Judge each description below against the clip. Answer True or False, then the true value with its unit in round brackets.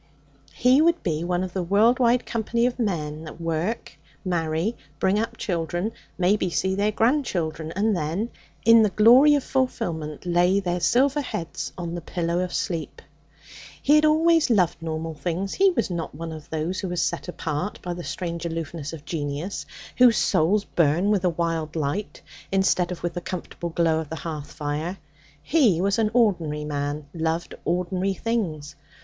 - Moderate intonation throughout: True (4.7 semitones)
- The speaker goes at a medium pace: True (175 wpm)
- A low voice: False (175 Hz)